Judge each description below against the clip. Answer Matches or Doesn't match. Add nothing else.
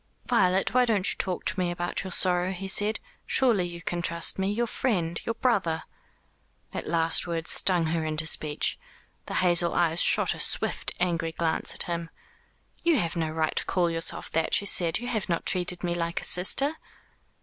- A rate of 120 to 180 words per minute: Doesn't match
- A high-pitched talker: Doesn't match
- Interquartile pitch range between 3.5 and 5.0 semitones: Doesn't match